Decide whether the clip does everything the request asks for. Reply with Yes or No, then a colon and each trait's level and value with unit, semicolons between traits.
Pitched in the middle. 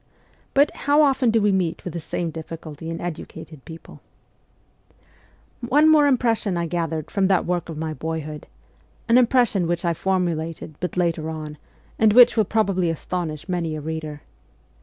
Yes: medium, 175 Hz